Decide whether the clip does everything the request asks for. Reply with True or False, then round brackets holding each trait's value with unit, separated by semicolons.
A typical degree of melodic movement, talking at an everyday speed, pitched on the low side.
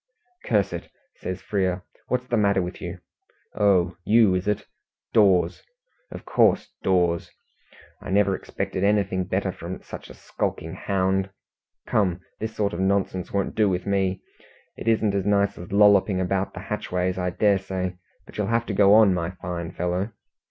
False (1.9 semitones; 165 wpm; 95 Hz)